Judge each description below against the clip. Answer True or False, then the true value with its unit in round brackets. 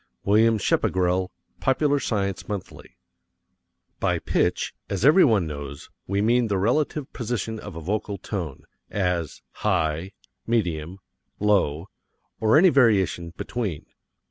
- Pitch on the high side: False (100 Hz)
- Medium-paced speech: False (115 wpm)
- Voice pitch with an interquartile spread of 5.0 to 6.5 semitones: False (4.5 semitones)